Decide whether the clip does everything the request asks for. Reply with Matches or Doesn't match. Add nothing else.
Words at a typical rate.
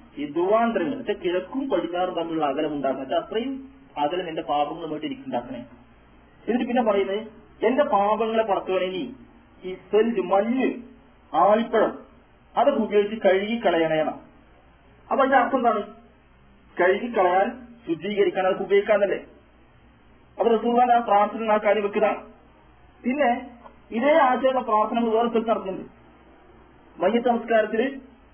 Matches